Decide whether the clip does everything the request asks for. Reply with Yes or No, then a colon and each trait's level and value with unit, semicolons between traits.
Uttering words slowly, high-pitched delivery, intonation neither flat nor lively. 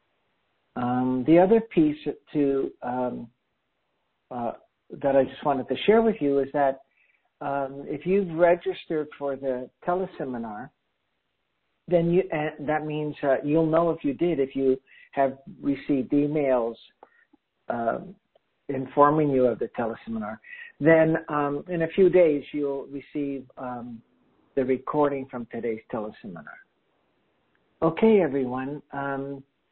No: slow, 130 wpm; medium, 145 Hz; average, 3.8 semitones